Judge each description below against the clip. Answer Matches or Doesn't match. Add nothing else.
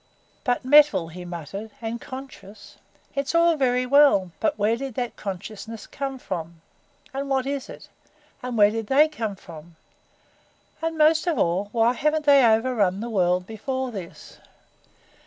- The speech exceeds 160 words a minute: Doesn't match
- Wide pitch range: Matches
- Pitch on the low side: Doesn't match